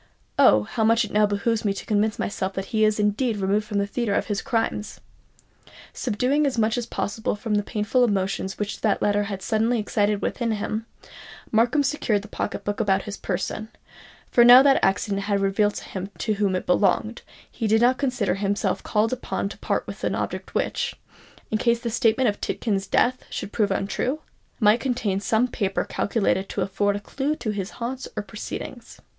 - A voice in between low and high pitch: No, high, 210 Hz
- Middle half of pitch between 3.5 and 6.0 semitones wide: No, average, 2.7 semitones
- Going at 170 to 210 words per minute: Yes, average, 195 wpm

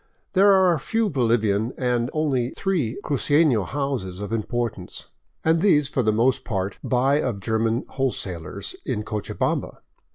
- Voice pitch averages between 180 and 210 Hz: No, low, 125 Hz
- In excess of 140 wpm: No, slow, 135 wpm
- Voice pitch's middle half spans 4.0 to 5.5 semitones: Yes, average, 5.2 semitones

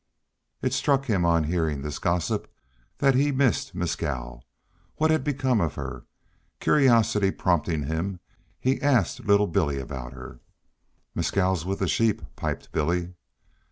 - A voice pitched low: Yes, very low, 90 Hz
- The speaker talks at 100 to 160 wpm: Yes, average, 140 wpm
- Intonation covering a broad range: Yes, wide, 7.7 semitones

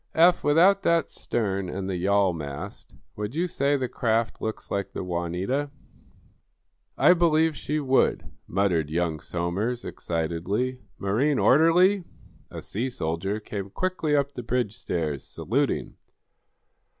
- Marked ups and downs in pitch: Yes, wide, 8.3 semitones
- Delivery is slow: Yes, slow, 130 wpm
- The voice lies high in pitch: No, low, 110 Hz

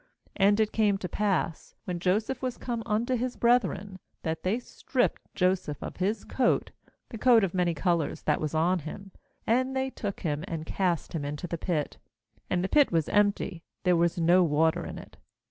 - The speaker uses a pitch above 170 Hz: Yes, medium, 185 Hz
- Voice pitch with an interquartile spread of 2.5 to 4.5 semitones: No, average, 4.9 semitones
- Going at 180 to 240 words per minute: Yes, average, 195 wpm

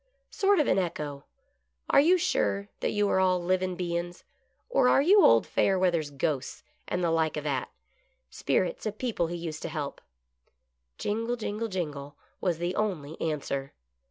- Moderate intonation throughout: No, wide, 5.7 semitones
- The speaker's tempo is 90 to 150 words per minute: No, average, 175 wpm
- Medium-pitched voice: Yes, medium, 175 Hz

